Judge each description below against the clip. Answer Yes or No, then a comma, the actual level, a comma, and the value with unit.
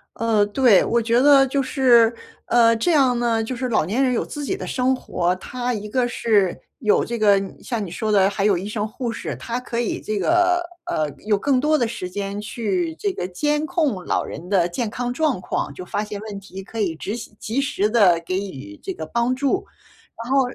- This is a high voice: Yes, high, 230 Hz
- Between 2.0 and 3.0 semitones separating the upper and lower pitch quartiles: No, average, 4.4 semitones